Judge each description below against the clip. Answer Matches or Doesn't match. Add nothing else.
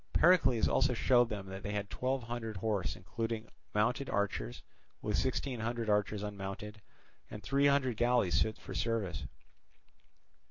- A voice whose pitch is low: Matches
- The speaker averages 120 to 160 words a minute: Matches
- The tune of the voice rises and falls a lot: Doesn't match